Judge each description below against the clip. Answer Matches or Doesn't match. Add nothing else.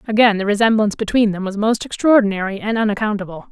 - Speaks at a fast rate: Doesn't match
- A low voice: Doesn't match